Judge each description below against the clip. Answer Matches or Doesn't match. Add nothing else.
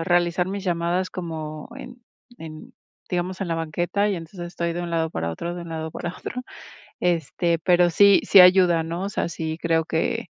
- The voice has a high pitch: Doesn't match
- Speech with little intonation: Matches